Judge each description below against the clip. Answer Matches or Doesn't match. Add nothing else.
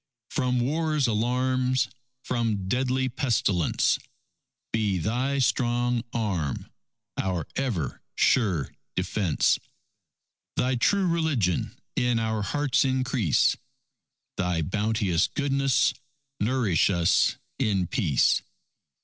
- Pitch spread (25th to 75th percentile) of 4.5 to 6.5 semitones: Matches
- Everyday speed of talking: Doesn't match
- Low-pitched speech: Matches